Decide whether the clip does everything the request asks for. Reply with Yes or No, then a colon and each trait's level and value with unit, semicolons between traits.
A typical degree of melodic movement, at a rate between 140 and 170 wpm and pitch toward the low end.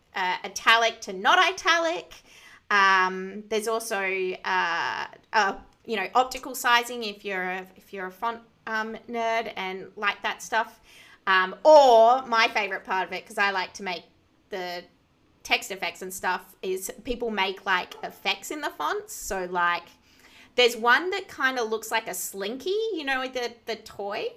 No: average, 4.2 semitones; average, 165 wpm; high, 220 Hz